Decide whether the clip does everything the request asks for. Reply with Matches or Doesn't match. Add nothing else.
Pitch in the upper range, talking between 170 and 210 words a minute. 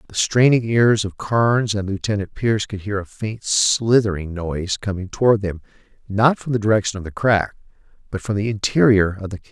Doesn't match